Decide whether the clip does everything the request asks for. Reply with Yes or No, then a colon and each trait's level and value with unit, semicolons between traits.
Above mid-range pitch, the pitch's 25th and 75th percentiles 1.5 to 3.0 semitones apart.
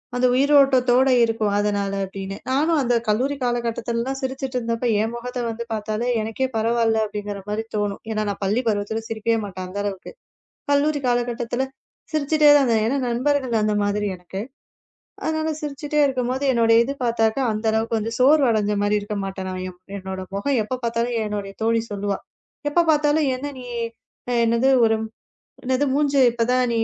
No: high, 235 Hz; average, 3.8 semitones